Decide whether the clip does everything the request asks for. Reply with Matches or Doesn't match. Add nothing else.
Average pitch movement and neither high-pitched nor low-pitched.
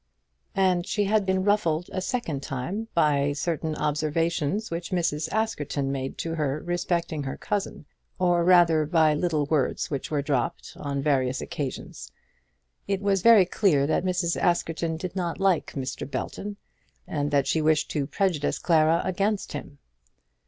Matches